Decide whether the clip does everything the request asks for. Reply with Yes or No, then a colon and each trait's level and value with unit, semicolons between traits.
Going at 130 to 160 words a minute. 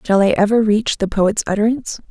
No: average, 200 wpm